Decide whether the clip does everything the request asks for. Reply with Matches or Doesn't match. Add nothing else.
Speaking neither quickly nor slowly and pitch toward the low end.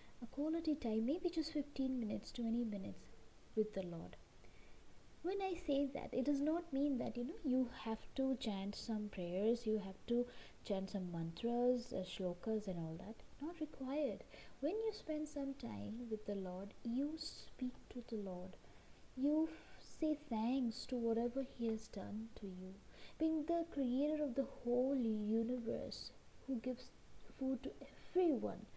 Doesn't match